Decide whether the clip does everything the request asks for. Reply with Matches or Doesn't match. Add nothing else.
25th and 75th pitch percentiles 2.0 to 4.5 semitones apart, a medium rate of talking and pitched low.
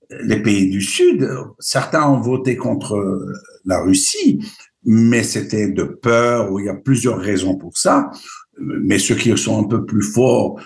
Doesn't match